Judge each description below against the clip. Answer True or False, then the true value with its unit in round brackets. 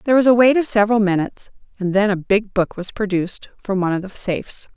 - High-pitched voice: True (205 Hz)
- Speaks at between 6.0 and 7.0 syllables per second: True (6.6 syllables/s)